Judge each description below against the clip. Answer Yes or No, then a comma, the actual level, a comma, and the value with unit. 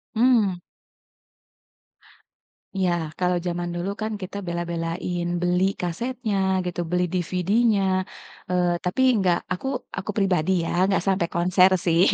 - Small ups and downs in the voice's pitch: Yes, narrow, 2.0 semitones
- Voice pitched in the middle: Yes, medium, 180 Hz